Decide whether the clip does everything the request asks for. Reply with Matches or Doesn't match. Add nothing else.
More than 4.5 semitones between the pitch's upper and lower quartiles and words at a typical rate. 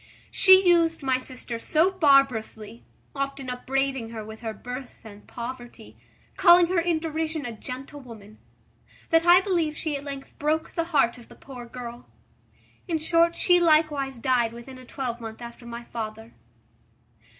Matches